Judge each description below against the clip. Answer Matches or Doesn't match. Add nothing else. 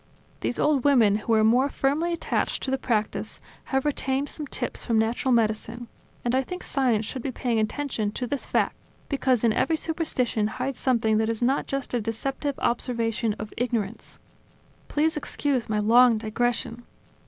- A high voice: Matches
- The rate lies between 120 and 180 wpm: Matches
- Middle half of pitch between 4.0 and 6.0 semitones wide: Doesn't match